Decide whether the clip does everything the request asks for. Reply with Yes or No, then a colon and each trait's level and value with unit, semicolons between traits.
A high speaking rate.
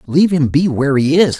Yes: fast, 260 wpm